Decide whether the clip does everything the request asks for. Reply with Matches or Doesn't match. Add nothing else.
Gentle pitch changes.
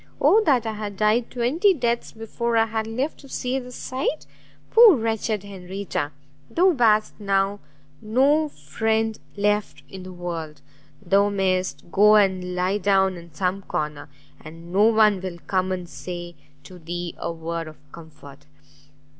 Doesn't match